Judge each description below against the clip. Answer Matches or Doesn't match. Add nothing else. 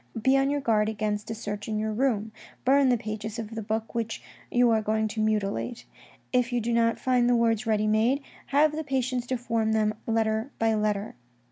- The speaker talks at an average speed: Doesn't match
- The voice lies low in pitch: Doesn't match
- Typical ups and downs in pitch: Doesn't match